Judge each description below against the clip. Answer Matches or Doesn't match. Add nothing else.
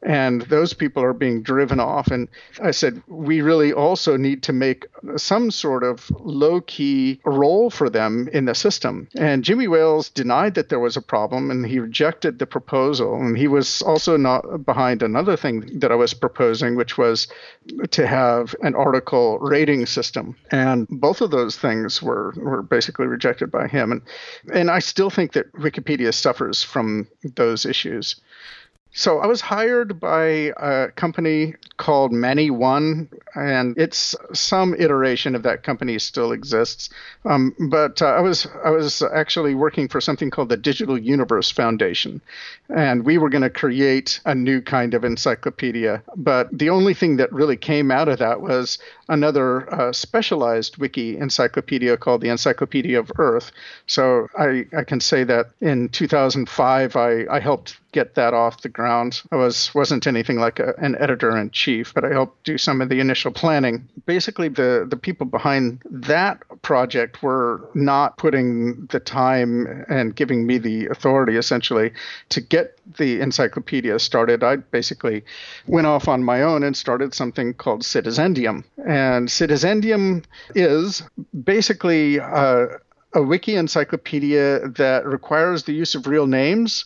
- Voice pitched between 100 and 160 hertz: Matches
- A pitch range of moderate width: Matches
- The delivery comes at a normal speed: Matches